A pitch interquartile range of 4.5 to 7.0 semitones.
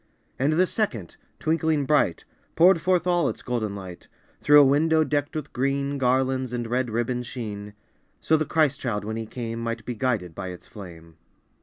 Yes: average, 5.3 semitones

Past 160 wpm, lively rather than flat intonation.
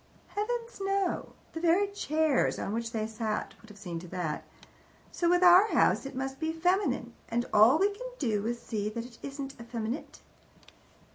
Yes: average, 185 wpm; wide, 8.1 semitones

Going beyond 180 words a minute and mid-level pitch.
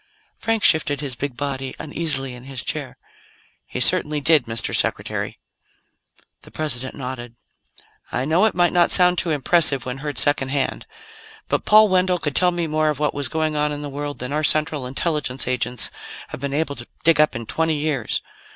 Yes: average, 190 wpm; medium, 145 Hz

